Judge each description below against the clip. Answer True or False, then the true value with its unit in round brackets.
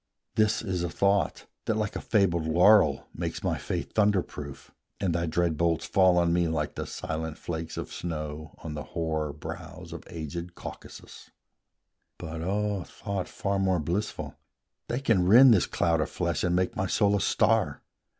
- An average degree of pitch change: True (3.6 semitones)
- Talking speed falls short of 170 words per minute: False (175 wpm)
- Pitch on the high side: False (85 Hz)